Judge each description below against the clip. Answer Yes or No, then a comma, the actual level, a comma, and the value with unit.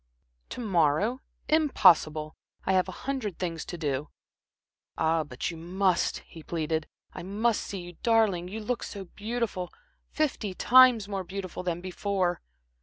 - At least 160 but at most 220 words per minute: No, average, 145 wpm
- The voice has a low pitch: No, medium, 185 Hz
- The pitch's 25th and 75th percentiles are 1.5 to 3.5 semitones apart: No, average, 4.5 semitones